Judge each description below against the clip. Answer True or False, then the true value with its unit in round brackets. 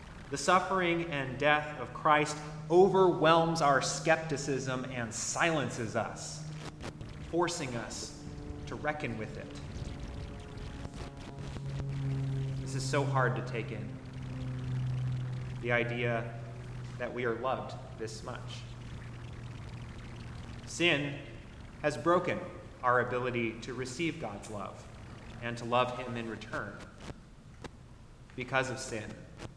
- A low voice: True (125 Hz)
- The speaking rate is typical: False (105 wpm)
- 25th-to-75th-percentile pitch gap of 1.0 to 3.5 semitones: True (3.2 semitones)